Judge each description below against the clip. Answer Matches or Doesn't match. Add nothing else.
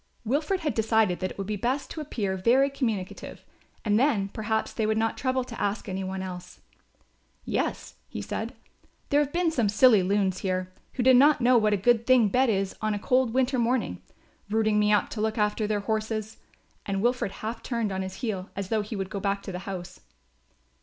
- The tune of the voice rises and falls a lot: Doesn't match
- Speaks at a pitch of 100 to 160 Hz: Doesn't match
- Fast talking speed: Matches